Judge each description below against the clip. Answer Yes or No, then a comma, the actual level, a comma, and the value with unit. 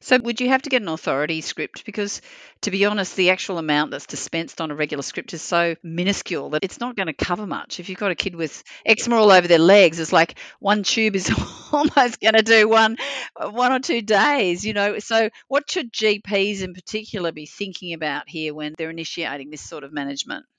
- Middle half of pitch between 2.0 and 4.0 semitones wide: No, average, 5.1 semitones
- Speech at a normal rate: No, fast, 220 wpm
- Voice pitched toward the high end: Yes, high, 195 Hz